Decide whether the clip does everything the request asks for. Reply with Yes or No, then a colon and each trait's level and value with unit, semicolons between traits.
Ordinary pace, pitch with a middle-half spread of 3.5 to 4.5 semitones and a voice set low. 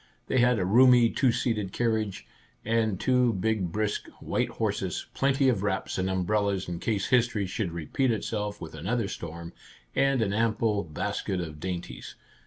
Yes: average, 160 wpm; average, 4.0 semitones; low, 105 Hz